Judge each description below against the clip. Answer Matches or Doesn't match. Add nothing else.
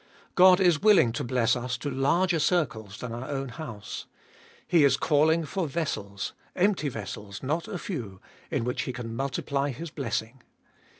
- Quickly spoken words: Doesn't match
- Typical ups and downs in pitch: Doesn't match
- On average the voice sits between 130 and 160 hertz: Matches